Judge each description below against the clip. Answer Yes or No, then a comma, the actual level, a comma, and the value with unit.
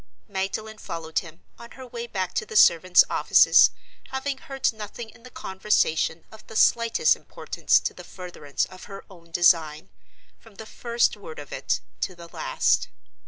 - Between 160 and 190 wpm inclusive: Yes, average, 165 wpm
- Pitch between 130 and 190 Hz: No, high, 205 Hz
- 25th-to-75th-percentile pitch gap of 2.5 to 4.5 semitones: No, average, 5.2 semitones